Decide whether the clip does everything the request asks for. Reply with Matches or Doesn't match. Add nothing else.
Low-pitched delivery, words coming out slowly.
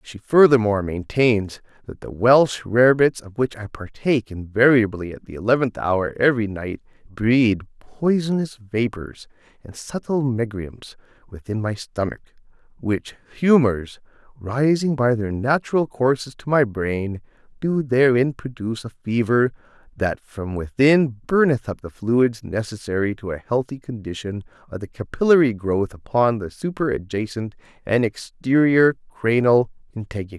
Matches